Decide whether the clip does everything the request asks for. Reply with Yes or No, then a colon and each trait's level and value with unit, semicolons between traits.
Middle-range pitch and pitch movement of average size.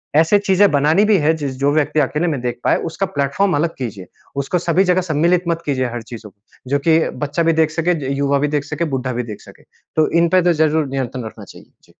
Yes: medium, 150 Hz; average, 3.5 semitones